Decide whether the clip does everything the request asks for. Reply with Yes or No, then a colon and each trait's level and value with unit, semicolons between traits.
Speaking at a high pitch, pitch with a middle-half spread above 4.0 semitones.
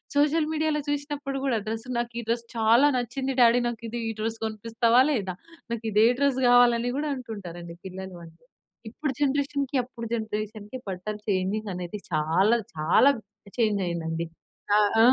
Yes: high, 230 Hz; average, 4.5 semitones